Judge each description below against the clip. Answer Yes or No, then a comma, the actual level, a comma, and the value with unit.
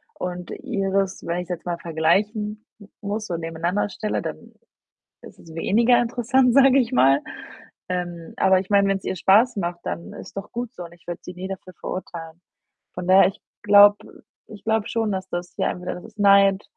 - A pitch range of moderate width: Yes, average, 3.3 semitones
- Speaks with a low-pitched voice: No, high, 195 Hz